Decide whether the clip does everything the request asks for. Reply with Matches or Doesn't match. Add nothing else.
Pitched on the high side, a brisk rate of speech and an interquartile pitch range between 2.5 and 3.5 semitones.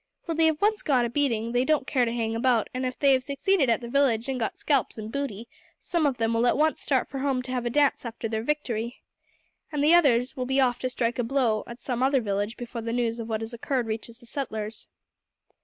Matches